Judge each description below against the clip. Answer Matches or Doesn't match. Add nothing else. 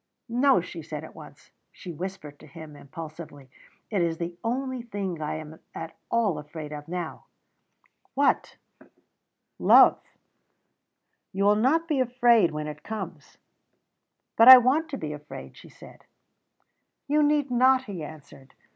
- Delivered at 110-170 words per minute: Matches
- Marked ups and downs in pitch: Matches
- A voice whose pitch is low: Doesn't match